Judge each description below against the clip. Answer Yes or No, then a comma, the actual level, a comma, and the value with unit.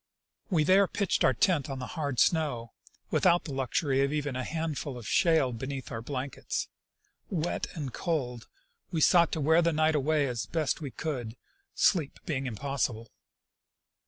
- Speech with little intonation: No, average, 3.9 semitones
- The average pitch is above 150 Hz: No, medium, 145 Hz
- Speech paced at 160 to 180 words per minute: Yes, average, 165 wpm